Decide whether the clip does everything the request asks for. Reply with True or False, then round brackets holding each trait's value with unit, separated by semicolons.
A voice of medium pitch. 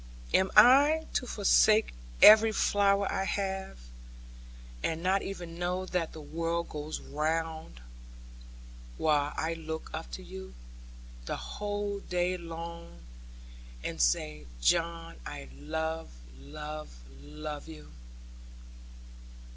True (165 Hz)